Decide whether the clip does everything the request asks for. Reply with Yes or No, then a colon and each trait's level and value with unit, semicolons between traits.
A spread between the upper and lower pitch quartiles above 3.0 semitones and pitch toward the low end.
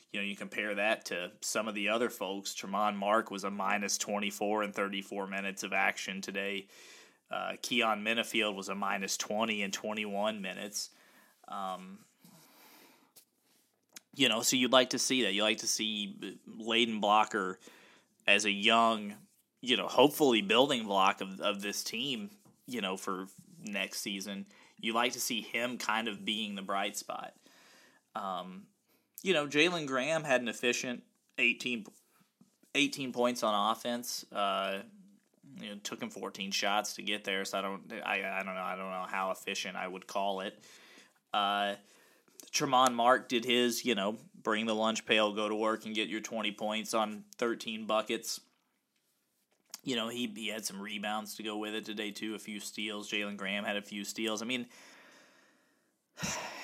No: average, 2.7 semitones; low, 105 Hz